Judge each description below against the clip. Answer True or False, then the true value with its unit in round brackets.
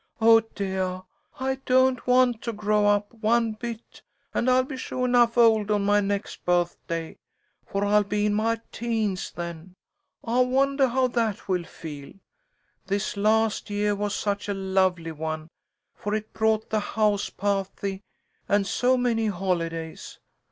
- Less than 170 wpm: True (150 wpm)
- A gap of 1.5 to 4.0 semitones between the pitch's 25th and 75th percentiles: True (3.3 semitones)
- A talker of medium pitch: False (210 Hz)